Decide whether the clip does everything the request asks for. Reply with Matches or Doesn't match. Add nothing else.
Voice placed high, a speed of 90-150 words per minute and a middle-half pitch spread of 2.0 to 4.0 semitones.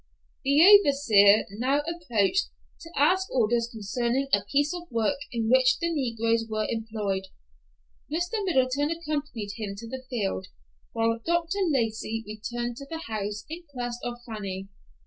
Doesn't match